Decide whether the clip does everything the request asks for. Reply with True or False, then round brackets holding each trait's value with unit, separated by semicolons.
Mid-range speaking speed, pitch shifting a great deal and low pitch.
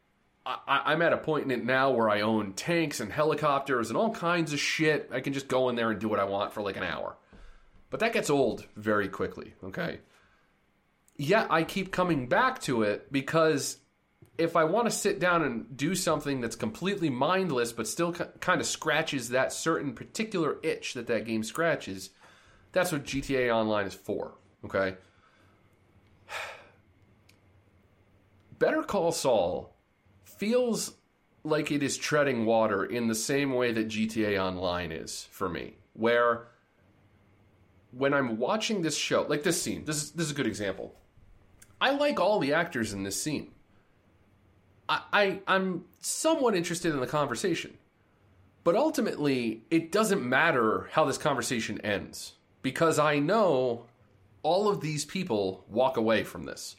True (160 wpm; 8.0 semitones; 130 Hz)